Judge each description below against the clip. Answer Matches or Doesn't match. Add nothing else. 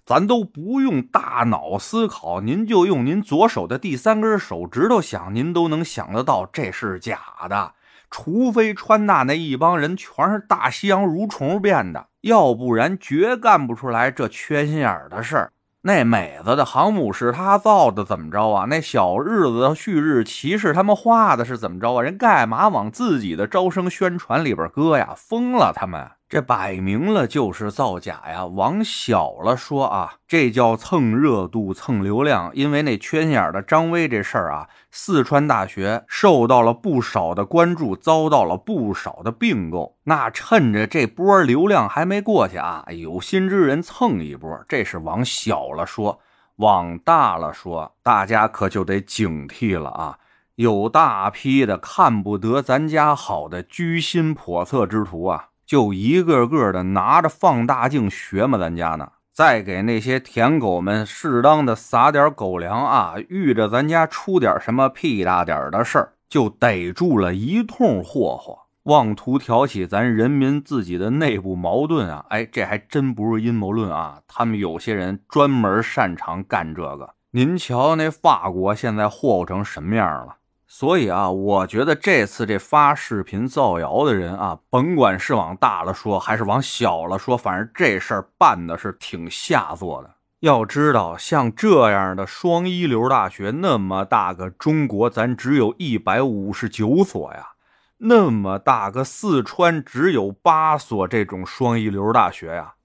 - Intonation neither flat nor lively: Doesn't match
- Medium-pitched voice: Doesn't match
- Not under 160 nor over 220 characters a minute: Doesn't match